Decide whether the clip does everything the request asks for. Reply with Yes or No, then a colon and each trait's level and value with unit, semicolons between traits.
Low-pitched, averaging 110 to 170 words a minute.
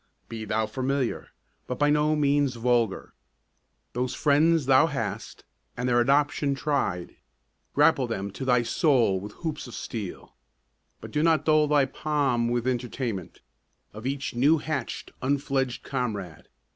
Yes: low, 130 Hz; average, 140 wpm